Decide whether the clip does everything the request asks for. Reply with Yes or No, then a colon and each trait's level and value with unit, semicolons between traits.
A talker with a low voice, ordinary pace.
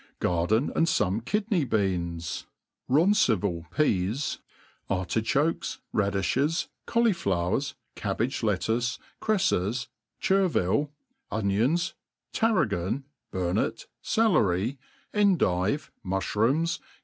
No: low, 115 Hz; slow, 75 wpm